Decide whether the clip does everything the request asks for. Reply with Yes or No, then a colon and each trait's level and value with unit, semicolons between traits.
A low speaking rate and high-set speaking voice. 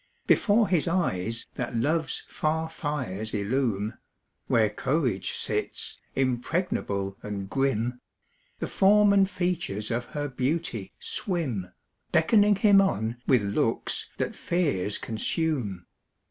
No: slow, 110 wpm; low, 135 Hz